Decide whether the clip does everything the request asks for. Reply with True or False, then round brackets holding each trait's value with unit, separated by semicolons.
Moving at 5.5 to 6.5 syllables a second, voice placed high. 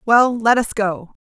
False (3.8 syllables/s; 220 Hz)